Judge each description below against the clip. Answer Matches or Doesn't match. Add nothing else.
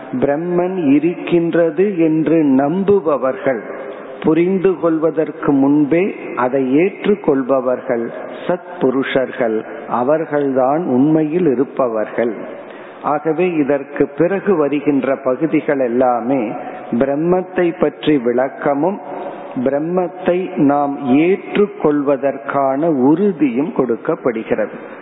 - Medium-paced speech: Doesn't match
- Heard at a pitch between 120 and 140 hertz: Doesn't match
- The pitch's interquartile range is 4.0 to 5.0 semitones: Matches